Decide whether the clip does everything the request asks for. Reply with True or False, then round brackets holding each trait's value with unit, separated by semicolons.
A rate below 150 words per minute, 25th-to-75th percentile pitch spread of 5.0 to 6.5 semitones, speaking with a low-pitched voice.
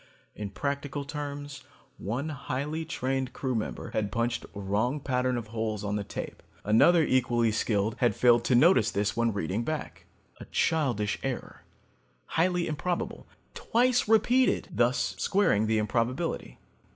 True (140 wpm; 5.3 semitones; 125 Hz)